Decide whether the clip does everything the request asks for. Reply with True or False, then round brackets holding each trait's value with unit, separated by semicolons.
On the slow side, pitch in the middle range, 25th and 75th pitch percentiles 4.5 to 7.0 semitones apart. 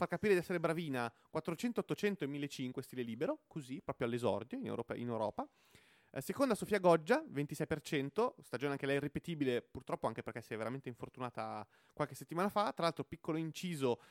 False (170 wpm; 145 Hz; 5.3 semitones)